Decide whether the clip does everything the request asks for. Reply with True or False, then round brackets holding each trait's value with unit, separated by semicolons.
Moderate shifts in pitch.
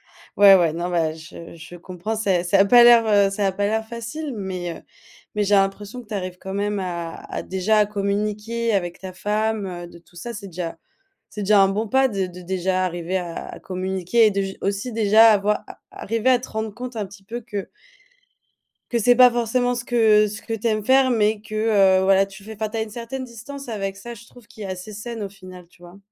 True (3.2 semitones)